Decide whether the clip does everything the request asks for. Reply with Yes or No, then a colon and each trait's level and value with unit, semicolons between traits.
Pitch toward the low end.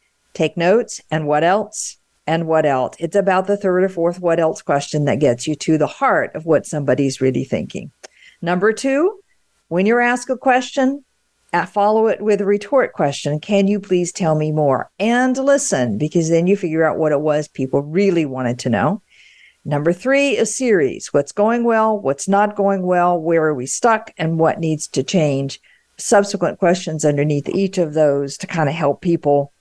No: medium, 175 Hz